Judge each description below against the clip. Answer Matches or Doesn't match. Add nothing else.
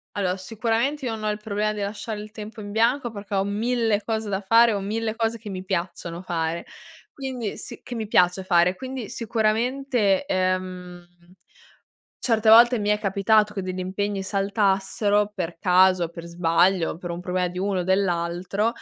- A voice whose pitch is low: Doesn't match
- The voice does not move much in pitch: Doesn't match